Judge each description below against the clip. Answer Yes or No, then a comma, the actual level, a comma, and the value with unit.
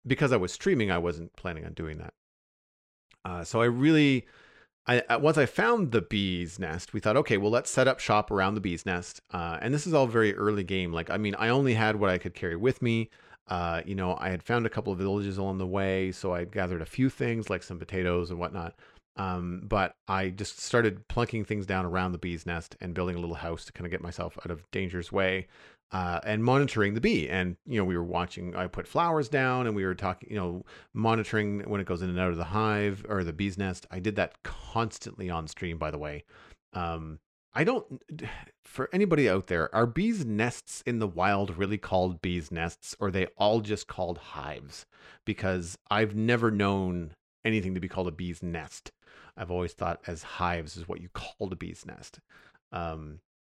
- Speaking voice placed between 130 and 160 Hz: No, very low, 95 Hz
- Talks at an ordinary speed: No, fast, 220 wpm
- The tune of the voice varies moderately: Yes, average, 3.6 semitones